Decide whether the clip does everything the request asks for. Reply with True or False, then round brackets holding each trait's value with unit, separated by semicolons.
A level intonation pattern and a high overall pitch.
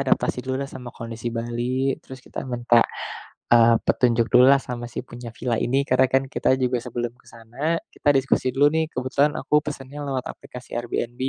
False (2.2 semitones; 125 Hz)